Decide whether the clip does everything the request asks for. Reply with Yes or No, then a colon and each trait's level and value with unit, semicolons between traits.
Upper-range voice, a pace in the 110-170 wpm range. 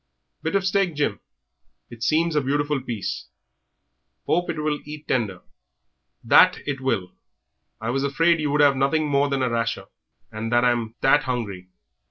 No: medium, 140 Hz; average, 160 wpm